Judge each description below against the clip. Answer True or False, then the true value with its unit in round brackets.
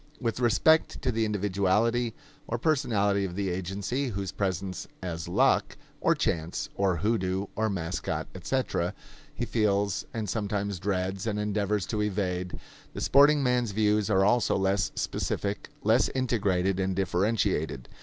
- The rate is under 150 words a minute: True (140 wpm)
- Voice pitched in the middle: False (100 Hz)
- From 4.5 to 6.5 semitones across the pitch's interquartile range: False (3.0 semitones)